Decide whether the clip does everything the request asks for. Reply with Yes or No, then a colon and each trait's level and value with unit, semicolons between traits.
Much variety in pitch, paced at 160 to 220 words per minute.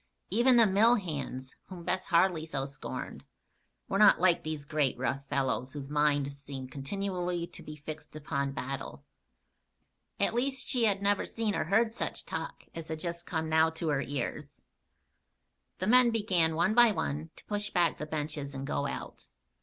Yes: wide, 5.7 semitones; average, 175 wpm